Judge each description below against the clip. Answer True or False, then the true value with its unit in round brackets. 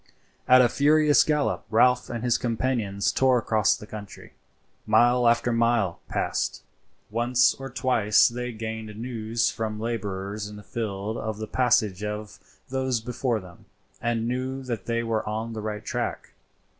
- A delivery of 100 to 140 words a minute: False (155 wpm)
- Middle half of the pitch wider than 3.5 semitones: False (2.6 semitones)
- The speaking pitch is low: True (115 Hz)